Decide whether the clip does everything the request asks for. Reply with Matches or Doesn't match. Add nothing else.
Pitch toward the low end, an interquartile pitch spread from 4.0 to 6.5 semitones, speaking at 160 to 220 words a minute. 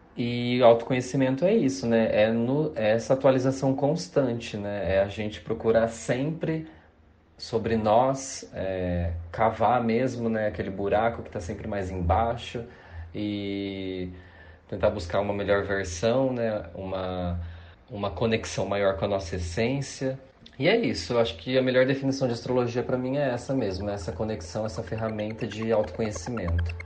Doesn't match